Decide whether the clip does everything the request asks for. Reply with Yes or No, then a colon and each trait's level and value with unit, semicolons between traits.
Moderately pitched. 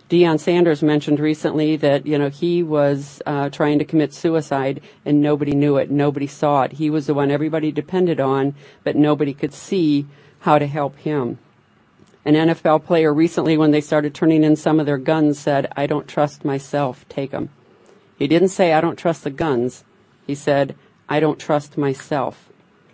Yes: medium, 150 Hz